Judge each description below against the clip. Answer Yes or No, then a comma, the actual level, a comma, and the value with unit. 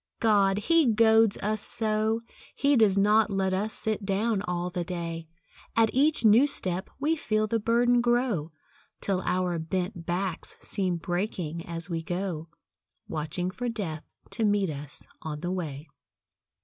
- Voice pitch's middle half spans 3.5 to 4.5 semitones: Yes, average, 4.1 semitones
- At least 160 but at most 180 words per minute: No, average, 150 wpm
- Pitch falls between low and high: No, high, 195 Hz